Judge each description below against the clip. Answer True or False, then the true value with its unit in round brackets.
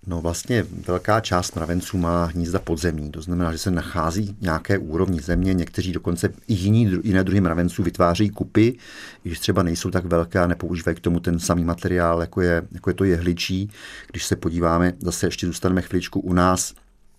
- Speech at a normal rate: False (180 wpm)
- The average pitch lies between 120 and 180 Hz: False (90 Hz)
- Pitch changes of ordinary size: False (1.9 semitones)